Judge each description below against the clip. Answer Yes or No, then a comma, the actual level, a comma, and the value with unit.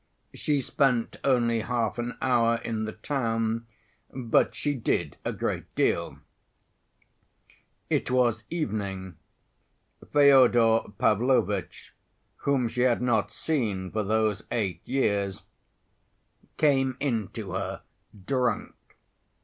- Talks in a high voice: No, low, 115 Hz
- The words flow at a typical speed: No, slow, 105 wpm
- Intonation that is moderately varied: Yes, average, 3.0 semitones